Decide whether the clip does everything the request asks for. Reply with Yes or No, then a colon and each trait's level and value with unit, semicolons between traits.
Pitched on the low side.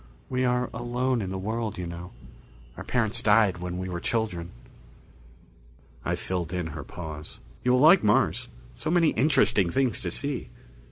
Yes: low, 110 Hz